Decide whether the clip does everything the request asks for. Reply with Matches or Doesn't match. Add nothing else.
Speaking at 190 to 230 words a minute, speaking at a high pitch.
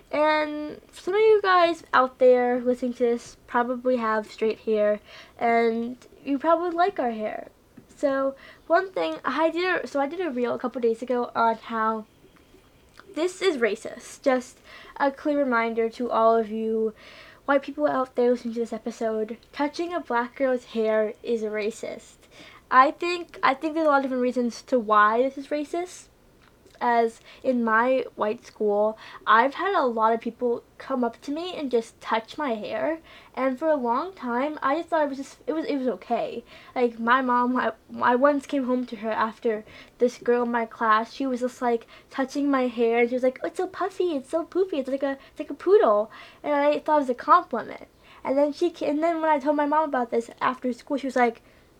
Matches